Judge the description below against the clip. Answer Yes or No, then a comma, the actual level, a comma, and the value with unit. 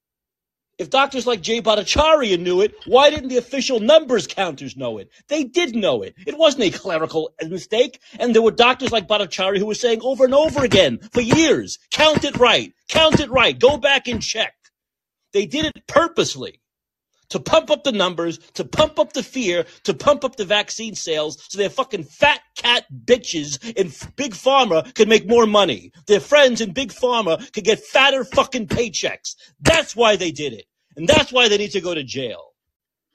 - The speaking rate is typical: Yes, average, 190 wpm